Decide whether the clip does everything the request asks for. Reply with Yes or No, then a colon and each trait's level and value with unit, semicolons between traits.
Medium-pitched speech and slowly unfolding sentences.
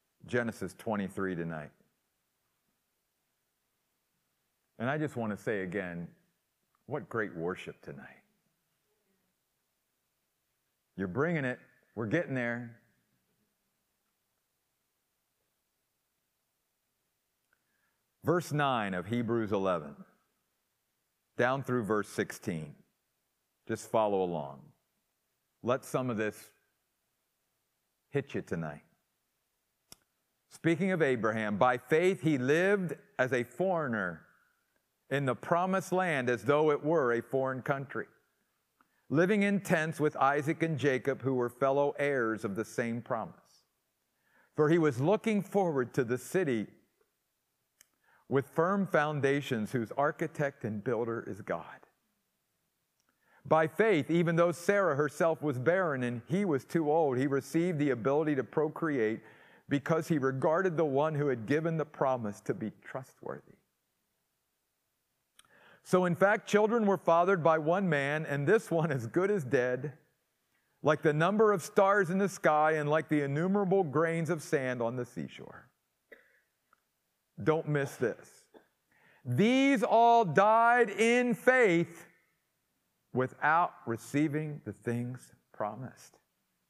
Yes: medium, 145 Hz; slow, 120 wpm